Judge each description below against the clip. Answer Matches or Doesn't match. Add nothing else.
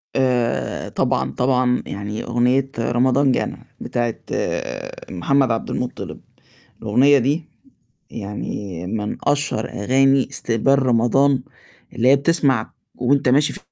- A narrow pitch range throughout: Doesn't match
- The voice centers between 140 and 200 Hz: Doesn't match